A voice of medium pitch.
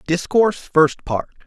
Yes: medium, 165 Hz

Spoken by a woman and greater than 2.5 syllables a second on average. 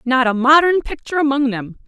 Yes: female; 5.8 syllables/s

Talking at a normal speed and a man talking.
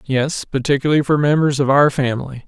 Yes: average, 170 wpm; male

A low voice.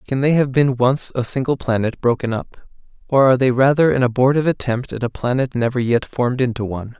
Yes: low, 125 Hz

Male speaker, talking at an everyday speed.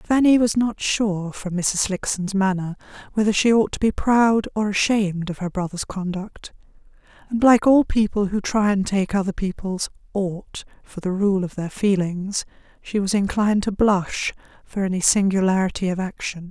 No: female; average, 170 wpm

